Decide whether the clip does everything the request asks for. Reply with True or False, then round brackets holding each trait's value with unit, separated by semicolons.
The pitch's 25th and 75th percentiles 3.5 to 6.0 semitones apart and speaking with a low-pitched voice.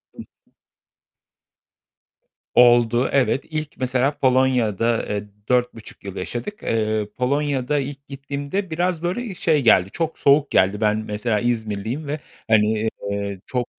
True (4.8 semitones; 125 Hz)